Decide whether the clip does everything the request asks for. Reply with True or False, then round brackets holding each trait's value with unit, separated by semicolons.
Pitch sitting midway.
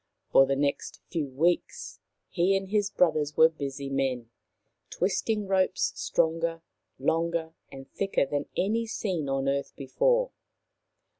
True (165 Hz)